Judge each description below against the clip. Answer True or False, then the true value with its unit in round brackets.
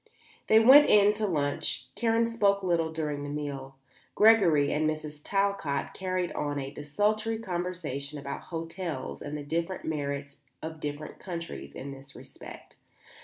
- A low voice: False (160 Hz)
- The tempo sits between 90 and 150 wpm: True (145 wpm)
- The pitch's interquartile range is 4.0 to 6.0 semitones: True (5.4 semitones)